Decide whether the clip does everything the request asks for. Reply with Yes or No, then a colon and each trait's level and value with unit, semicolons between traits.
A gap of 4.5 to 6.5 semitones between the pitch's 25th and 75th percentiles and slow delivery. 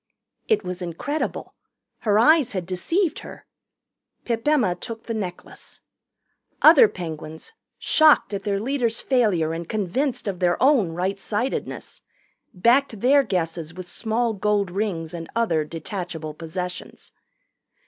Yes: wide, 5.5 semitones; slow, 130 wpm